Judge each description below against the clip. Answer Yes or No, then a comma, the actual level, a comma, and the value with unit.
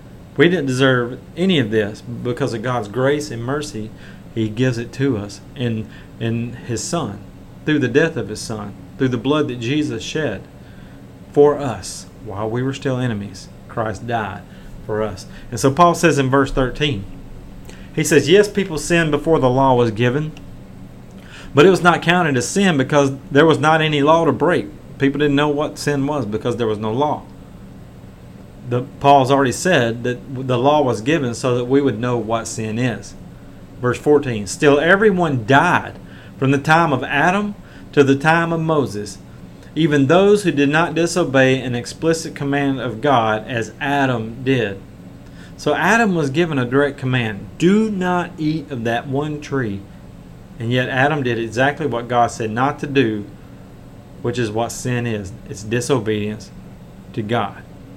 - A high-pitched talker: No, low, 135 Hz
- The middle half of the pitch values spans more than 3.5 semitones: Yes, average, 4.4 semitones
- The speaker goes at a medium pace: Yes, average, 175 wpm